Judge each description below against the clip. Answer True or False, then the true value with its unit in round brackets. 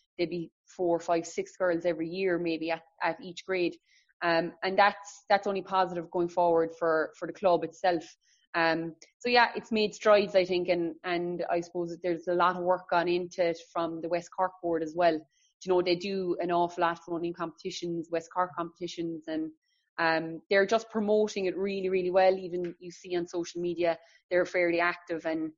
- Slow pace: False (205 wpm)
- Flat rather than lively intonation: True (1.8 semitones)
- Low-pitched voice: False (175 Hz)